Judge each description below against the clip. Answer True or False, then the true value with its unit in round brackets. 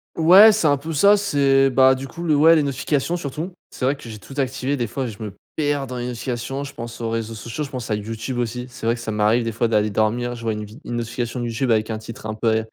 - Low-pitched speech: True (125 Hz)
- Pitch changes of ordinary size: True (3.7 semitones)